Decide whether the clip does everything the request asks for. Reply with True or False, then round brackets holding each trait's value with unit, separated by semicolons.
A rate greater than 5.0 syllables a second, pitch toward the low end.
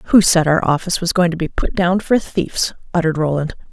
False (5.9 syllables/s; 170 Hz)